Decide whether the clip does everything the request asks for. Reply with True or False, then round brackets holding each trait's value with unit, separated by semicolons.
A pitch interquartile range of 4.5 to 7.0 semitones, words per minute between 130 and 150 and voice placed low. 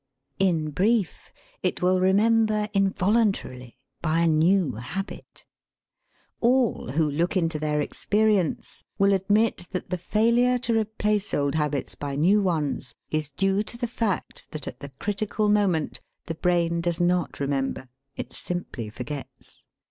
False (5.4 semitones; 140 wpm; 180 Hz)